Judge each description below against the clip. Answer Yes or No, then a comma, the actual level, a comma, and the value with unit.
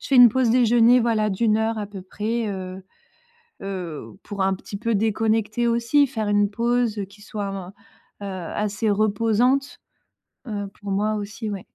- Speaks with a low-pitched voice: No, high, 215 Hz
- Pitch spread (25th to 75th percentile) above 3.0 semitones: No, narrow, 2.5 semitones